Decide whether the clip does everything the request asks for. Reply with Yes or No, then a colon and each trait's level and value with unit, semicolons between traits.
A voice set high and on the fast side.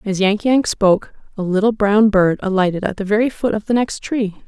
Yes: high, 205 Hz; fast, 230 wpm